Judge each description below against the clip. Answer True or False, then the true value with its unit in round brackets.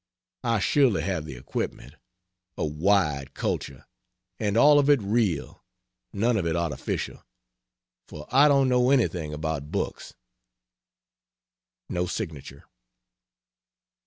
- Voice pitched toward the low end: True (95 Hz)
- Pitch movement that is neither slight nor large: False (8.2 semitones)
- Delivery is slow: True (110 wpm)